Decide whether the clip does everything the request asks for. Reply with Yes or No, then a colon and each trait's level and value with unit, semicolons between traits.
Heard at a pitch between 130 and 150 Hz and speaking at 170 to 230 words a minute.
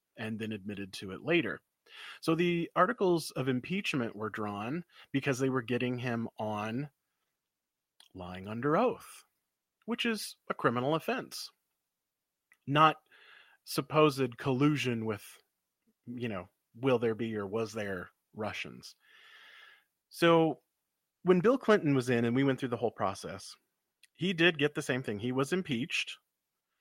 No: low, 135 Hz; average, 140 wpm